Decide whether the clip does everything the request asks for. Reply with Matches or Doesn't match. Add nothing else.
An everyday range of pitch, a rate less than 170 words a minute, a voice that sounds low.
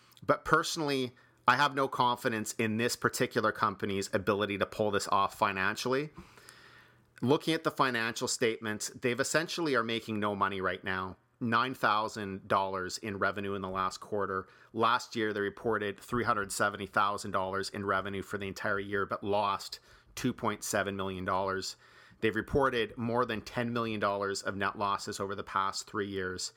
Matches